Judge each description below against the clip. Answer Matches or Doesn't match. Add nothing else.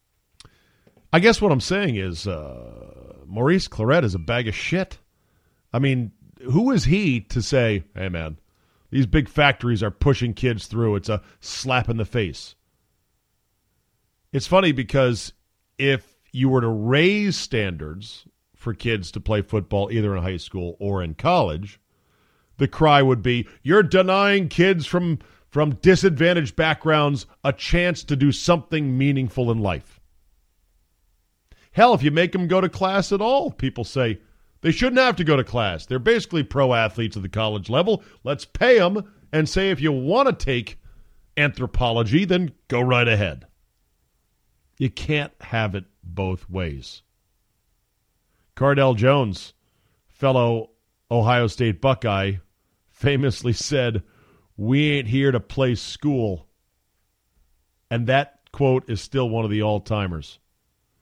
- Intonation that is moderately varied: Doesn't match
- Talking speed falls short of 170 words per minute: Matches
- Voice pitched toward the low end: Matches